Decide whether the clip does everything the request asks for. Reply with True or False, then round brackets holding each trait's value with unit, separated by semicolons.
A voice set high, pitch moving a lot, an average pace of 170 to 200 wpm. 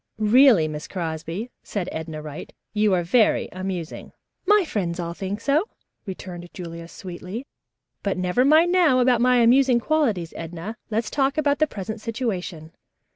False (210 Hz; 6.5 semitones; 150 wpm)